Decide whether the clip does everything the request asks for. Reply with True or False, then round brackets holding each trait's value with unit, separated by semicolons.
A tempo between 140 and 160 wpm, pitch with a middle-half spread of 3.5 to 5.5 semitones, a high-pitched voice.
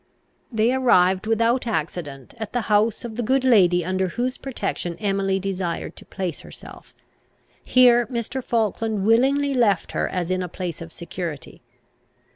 True (150 wpm; 4.8 semitones; 210 Hz)